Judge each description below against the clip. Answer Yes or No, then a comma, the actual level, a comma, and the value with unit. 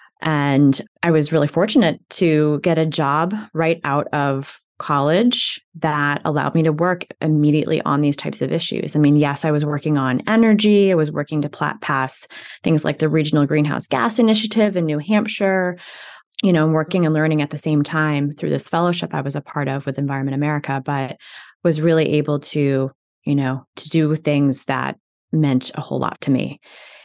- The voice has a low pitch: No, medium, 155 Hz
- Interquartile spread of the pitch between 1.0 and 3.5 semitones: Yes, narrow, 2.4 semitones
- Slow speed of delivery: No, average, 185 wpm